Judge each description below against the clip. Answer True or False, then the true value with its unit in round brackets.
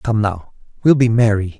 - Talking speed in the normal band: True (190 wpm)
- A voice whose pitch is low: True (110 Hz)